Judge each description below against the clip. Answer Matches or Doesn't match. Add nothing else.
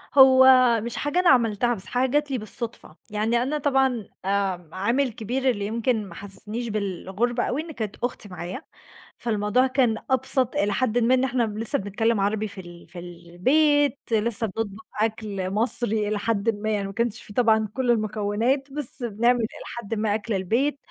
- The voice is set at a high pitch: Matches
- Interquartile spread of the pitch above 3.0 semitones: Matches